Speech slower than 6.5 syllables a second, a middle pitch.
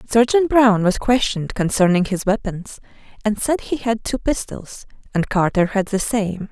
No: 4.6 syllables/s; high, 210 Hz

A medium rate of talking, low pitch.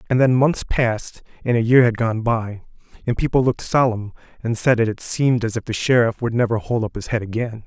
No: fast, 235 wpm; low, 115 Hz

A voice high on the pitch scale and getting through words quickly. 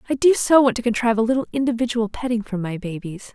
Yes: high, 235 Hz; fast, 235 wpm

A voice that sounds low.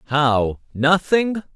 No: medium, 155 Hz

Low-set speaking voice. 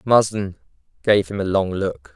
Yes: low, 100 Hz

